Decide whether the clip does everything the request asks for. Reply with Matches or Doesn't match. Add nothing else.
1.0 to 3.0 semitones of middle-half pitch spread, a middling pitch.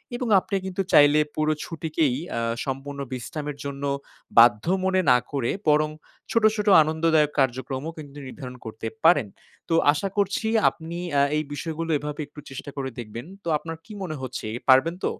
Doesn't match